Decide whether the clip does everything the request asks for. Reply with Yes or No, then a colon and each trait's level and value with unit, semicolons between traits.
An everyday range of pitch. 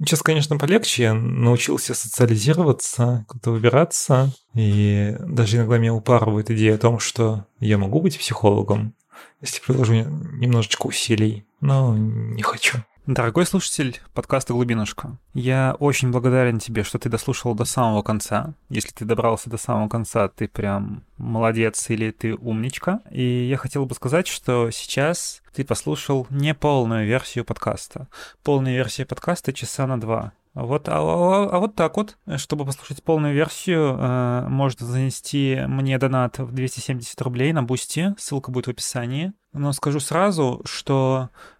Yes: average, 3.8 semitones